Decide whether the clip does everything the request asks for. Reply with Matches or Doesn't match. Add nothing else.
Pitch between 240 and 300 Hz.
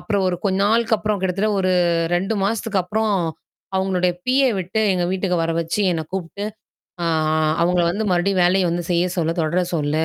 Doesn't match